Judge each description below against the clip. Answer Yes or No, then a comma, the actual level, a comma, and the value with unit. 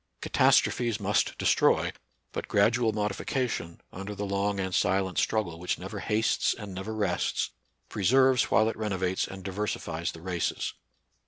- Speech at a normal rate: Yes, average, 150 wpm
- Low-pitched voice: Yes, low, 100 Hz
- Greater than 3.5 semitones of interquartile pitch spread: No, narrow, 2.6 semitones